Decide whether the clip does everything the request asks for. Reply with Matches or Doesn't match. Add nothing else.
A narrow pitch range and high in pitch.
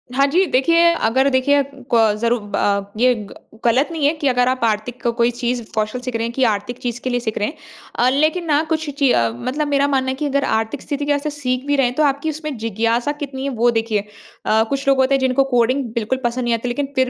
Doesn't match